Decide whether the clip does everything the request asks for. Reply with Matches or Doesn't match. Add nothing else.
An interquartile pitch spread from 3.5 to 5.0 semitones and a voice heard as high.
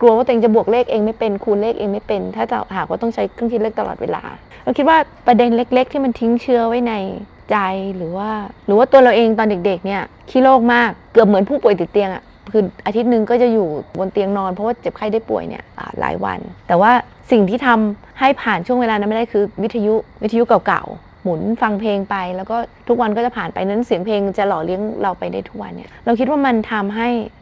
Doesn't match